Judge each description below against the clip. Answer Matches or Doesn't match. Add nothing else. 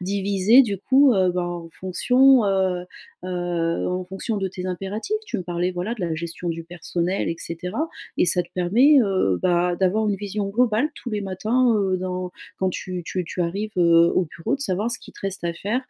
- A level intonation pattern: Doesn't match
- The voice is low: Doesn't match